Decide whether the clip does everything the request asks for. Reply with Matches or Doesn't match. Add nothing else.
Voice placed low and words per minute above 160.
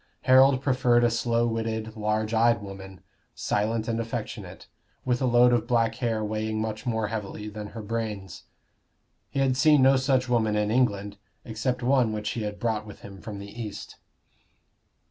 Matches